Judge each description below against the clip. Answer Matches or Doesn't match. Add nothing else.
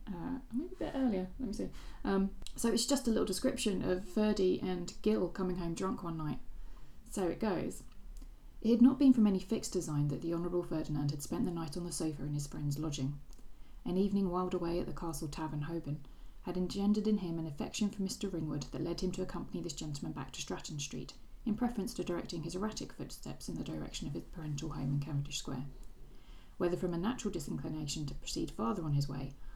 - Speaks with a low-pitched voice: Doesn't match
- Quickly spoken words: Matches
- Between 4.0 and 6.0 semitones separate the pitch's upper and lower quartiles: Matches